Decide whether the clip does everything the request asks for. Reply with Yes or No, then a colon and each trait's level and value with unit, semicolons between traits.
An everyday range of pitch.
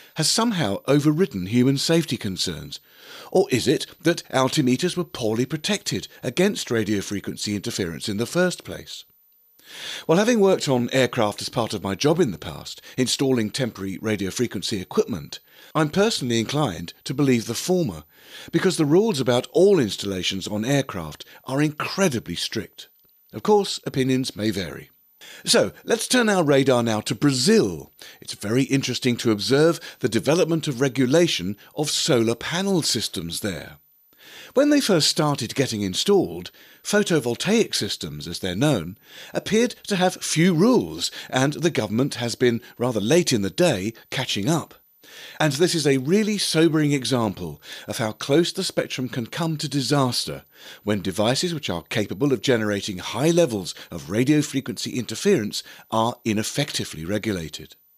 No: wide, 7.1 semitones